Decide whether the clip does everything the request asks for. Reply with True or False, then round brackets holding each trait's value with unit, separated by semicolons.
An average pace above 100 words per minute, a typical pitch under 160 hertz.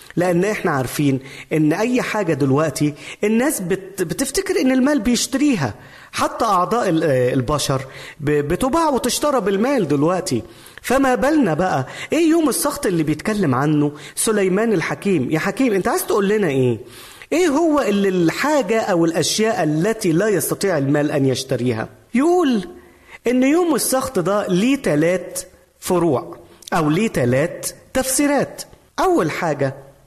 False (125 wpm; 185 Hz)